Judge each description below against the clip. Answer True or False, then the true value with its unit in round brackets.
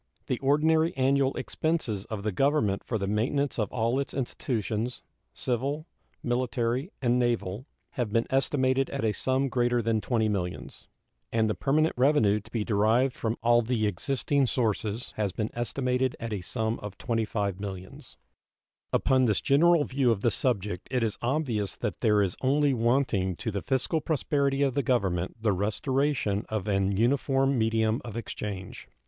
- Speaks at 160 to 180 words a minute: True (165 wpm)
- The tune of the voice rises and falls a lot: False (4.2 semitones)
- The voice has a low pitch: True (120 Hz)